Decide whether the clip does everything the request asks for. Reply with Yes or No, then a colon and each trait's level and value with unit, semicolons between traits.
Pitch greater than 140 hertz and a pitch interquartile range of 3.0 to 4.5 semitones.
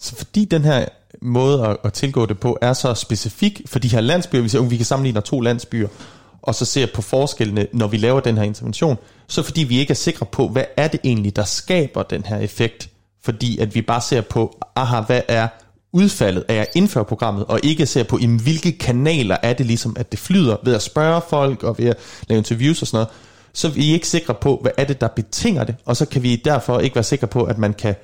No: low, 120 Hz; average, 3.7 semitones